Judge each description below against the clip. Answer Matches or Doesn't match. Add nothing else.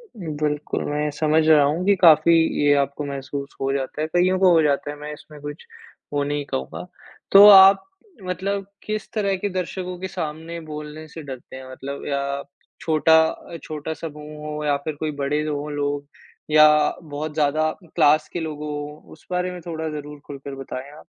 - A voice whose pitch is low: Doesn't match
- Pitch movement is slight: Matches